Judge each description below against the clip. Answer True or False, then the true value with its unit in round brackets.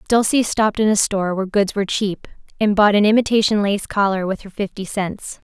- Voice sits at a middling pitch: False (205 Hz)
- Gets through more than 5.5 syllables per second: True (5.8 syllables/s)